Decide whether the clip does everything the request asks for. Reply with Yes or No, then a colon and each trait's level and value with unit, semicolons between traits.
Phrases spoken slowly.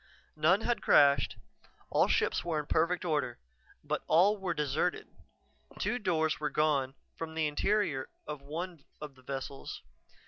No: average, 145 wpm